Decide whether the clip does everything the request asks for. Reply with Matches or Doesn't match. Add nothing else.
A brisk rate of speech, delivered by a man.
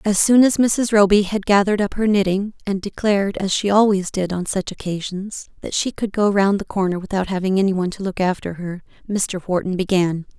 Doesn't match